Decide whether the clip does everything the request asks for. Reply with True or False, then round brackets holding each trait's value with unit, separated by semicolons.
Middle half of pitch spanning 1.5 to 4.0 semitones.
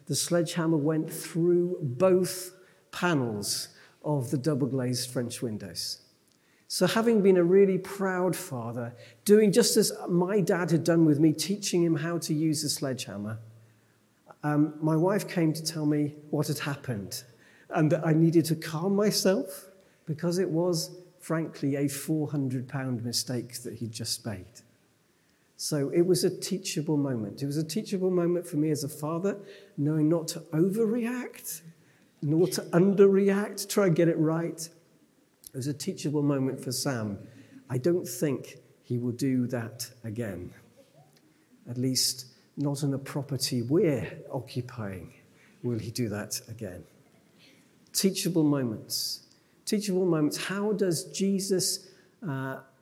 False (5.6 semitones)